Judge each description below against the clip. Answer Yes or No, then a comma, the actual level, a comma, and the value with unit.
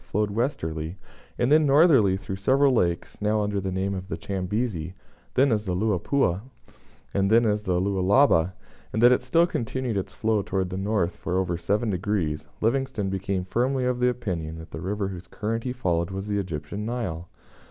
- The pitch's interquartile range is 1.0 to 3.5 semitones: No, average, 4.4 semitones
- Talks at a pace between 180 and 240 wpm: Yes, average, 185 wpm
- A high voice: No, low, 100 Hz